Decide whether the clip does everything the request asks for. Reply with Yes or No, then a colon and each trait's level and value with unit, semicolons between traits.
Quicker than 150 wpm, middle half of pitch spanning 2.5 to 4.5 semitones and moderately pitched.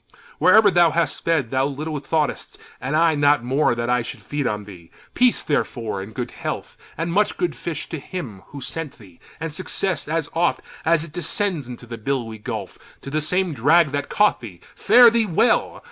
No: average, 195 wpm; wide, 5.5 semitones; medium, 150 Hz